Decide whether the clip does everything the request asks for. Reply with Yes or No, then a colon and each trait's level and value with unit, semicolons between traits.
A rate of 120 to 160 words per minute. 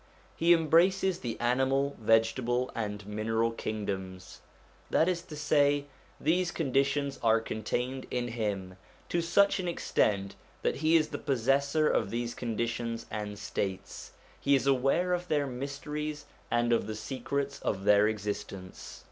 Yes: average, 140 wpm